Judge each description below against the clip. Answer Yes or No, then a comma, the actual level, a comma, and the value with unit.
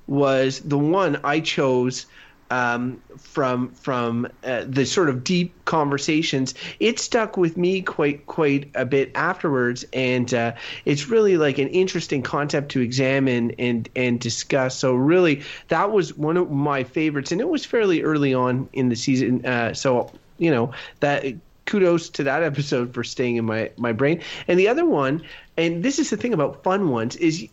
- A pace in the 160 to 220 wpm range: Yes, average, 175 wpm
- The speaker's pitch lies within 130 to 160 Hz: Yes, medium, 140 Hz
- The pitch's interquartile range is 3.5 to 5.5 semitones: Yes, average, 4.7 semitones